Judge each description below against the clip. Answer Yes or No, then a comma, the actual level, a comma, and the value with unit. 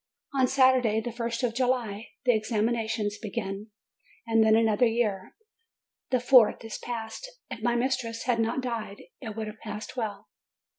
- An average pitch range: No, narrow, 2.1 semitones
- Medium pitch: No, high, 230 Hz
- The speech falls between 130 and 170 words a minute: Yes, average, 165 wpm